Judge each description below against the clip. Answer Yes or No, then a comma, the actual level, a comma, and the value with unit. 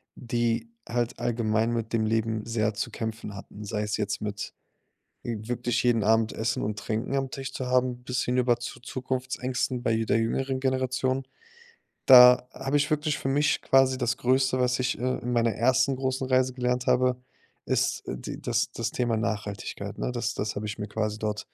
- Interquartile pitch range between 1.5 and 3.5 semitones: Yes, narrow, 2.6 semitones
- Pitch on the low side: Yes, low, 120 Hz